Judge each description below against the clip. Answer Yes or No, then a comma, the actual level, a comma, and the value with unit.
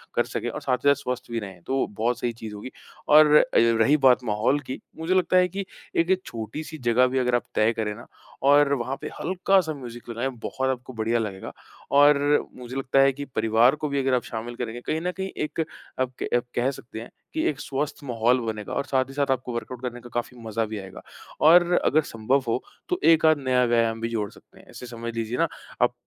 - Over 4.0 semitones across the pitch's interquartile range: No, average, 3.7 semitones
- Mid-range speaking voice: No, low, 125 Hz